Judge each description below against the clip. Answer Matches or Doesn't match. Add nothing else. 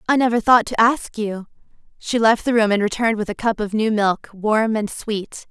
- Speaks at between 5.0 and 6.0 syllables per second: Matches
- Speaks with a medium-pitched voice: Doesn't match